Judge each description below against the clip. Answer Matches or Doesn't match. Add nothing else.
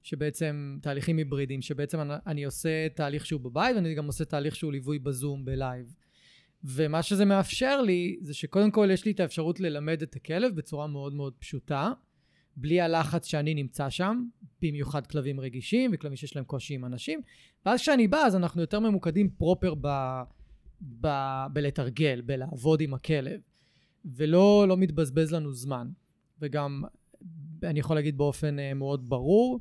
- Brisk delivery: Matches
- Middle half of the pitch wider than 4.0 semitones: Doesn't match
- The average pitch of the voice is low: Doesn't match